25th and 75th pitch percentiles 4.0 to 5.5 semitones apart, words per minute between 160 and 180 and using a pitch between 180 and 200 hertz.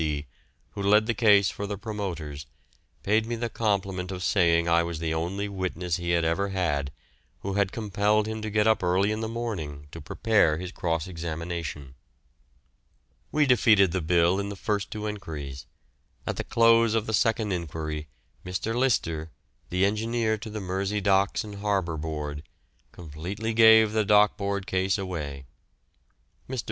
No: average, 4.3 semitones; average, 165 wpm; very low, 95 Hz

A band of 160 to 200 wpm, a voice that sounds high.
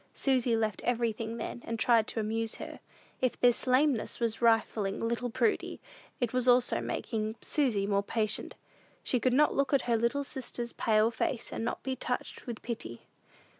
Yes: average, 170 wpm; high, 235 Hz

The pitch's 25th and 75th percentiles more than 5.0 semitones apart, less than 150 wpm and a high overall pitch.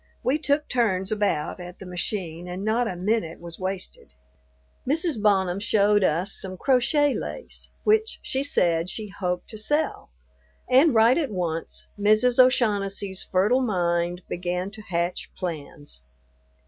Yes: wide, 5.4 semitones; average, 140 wpm; high, 200 Hz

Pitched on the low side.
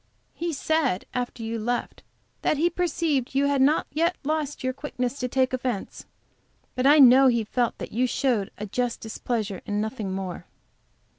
No: very high, 255 Hz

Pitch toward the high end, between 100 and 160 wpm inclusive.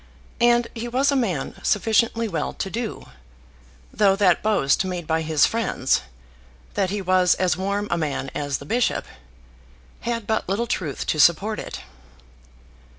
Yes: high, 195 Hz; average, 150 wpm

